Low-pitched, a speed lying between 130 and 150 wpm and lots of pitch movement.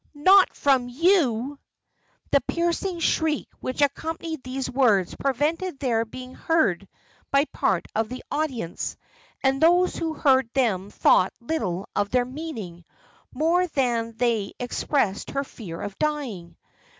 No: very high, 260 Hz; slow, 135 wpm; wide, 5.7 semitones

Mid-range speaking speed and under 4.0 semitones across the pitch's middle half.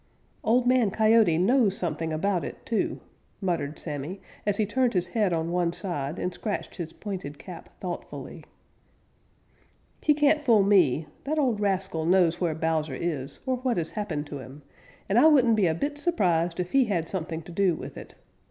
No: average, 180 wpm; average, 5.3 semitones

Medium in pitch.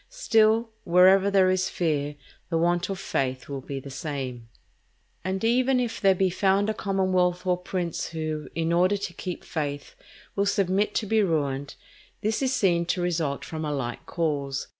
Yes: medium, 180 Hz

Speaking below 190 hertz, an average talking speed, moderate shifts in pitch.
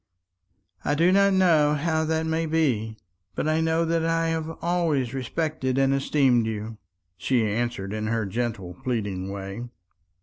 No: low, 135 Hz; average, 155 wpm; wide, 6.4 semitones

